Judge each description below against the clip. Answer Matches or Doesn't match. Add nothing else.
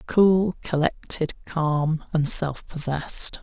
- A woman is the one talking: Doesn't match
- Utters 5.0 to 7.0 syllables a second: Doesn't match